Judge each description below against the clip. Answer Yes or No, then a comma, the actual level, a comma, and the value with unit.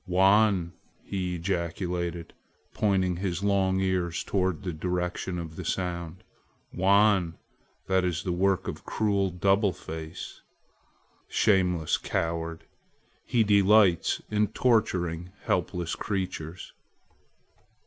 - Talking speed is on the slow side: Yes, slow, 100 wpm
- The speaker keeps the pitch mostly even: Yes, narrow, 2.3 semitones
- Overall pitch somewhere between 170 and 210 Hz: No, very low, 90 Hz